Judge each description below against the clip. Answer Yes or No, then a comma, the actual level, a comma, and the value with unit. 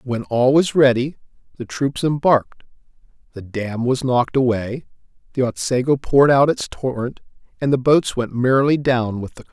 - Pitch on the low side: Yes, low, 130 Hz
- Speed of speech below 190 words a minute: Yes, average, 170 wpm